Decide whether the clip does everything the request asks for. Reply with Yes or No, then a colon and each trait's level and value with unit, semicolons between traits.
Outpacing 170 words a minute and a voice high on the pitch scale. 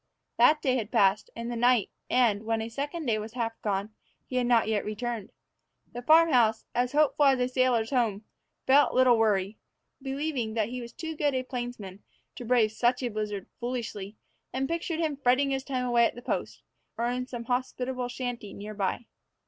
Yes: average, 195 wpm; high, 245 Hz